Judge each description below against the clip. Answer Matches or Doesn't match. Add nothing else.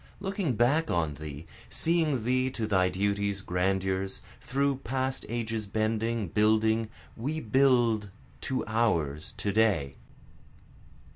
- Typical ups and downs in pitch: Matches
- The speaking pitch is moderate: Doesn't match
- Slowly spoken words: Matches